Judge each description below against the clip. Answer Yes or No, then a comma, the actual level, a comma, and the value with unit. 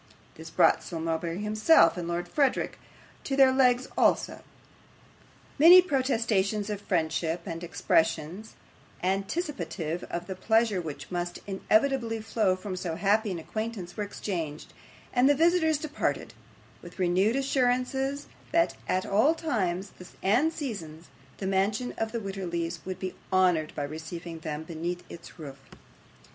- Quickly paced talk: No, slow, 135 wpm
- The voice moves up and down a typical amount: No, wide, 6.2 semitones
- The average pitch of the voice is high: Yes, high, 195 Hz